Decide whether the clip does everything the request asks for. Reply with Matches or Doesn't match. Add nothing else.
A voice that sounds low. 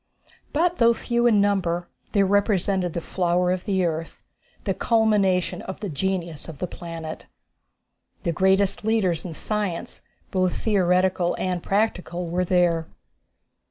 Doesn't match